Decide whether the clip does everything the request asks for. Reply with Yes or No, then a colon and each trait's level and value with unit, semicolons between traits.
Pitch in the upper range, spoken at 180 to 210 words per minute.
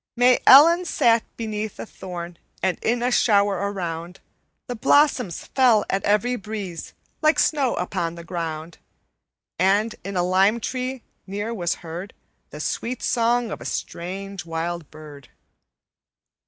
No: high, 200 Hz; average, 140 wpm